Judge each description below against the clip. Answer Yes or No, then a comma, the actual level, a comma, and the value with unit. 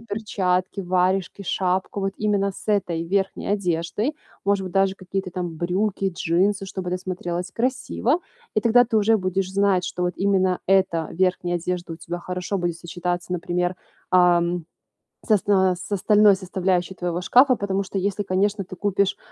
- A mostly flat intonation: Yes, narrow, 2.1 semitones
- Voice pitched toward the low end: No, high, 190 Hz